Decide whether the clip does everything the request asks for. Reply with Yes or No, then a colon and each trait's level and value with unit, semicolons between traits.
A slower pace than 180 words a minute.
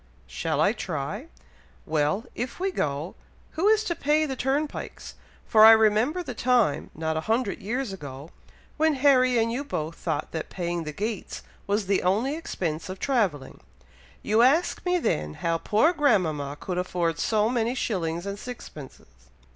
Yes: average, 165 wpm